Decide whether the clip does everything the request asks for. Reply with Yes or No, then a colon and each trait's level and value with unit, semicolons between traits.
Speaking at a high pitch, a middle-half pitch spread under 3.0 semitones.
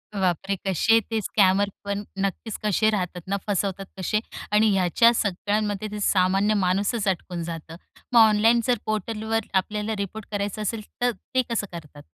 Yes: high, 205 Hz; narrow, 2.4 semitones